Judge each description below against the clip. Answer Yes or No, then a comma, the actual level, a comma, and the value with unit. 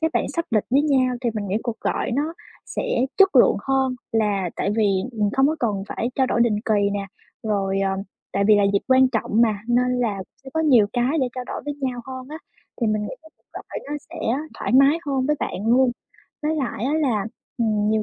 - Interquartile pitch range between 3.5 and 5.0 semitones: Yes, average, 4.3 semitones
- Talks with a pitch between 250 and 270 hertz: No, high, 240 Hz